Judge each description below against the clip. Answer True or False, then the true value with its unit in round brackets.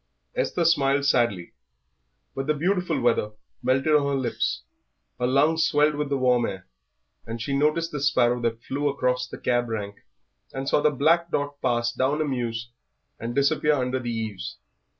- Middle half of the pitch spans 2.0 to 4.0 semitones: True (3.6 semitones)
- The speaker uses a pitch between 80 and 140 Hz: True (135 Hz)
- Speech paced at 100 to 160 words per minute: False (170 wpm)